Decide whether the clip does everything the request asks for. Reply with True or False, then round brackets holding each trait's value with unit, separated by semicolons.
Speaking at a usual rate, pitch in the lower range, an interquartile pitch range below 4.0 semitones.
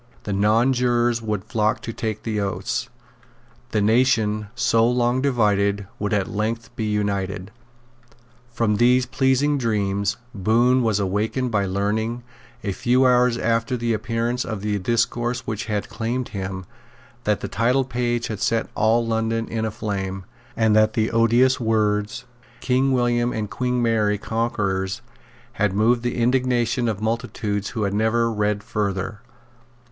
True (145 wpm; 115 Hz; 2.5 semitones)